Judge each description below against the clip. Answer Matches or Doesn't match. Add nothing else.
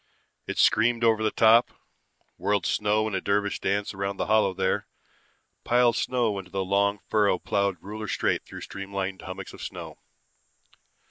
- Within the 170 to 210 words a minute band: Doesn't match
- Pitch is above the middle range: Doesn't match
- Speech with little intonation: Matches